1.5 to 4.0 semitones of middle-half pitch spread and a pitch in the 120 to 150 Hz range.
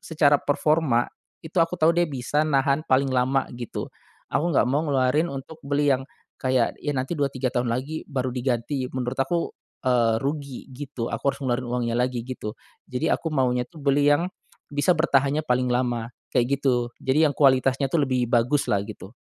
Yes: average, 2.8 semitones; low, 135 Hz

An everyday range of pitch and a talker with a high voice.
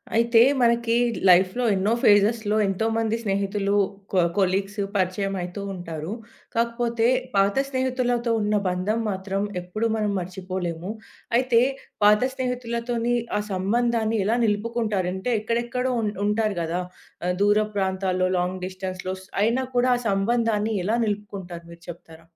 Yes: average, 3.7 semitones; high, 205 Hz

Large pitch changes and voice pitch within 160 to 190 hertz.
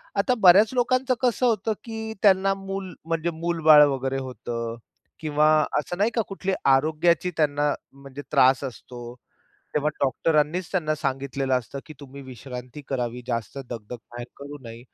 No: wide, 5.9 semitones; medium, 150 Hz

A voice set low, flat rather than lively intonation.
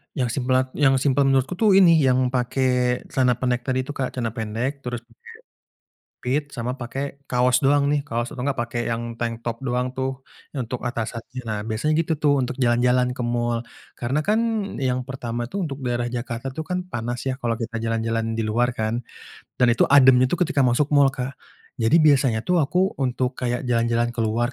Yes: low, 125 Hz; narrow, 2.3 semitones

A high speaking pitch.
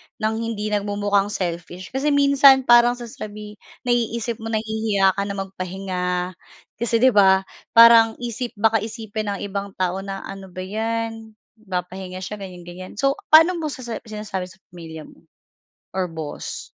Yes: high, 210 Hz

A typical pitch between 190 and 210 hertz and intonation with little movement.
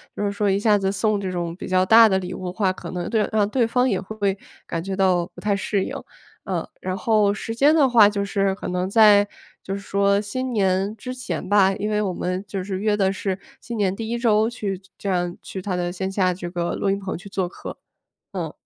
Yes: high, 200 Hz; narrow, 2.2 semitones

